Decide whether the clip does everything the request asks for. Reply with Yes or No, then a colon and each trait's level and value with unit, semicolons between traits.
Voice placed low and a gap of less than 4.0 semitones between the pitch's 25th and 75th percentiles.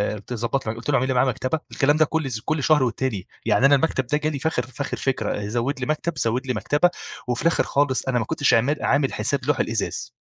Yes: low, 130 Hz; average, 3.4 semitones